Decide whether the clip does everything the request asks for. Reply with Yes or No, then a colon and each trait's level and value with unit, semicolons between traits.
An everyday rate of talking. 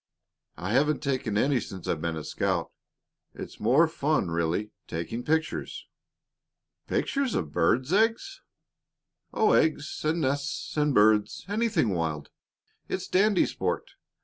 No: slow, 125 wpm